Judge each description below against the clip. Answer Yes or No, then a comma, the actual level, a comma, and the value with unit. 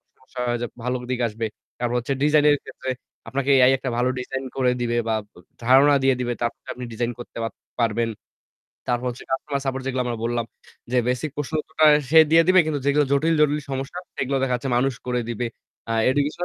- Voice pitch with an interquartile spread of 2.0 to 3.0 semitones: Yes, average, 2.7 semitones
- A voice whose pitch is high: No, low, 130 Hz